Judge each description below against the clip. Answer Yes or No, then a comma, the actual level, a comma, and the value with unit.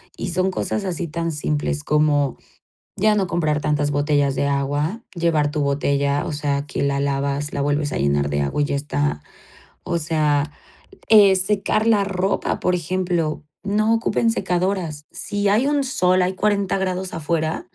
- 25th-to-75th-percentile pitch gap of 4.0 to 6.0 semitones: Yes, average, 4.7 semitones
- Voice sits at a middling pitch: Yes, medium, 155 Hz